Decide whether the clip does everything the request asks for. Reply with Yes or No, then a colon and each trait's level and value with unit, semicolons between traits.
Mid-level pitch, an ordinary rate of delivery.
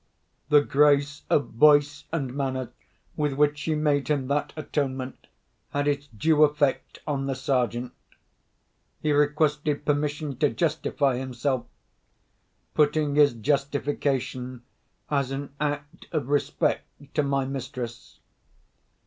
No: medium, 145 Hz; slow, 115 wpm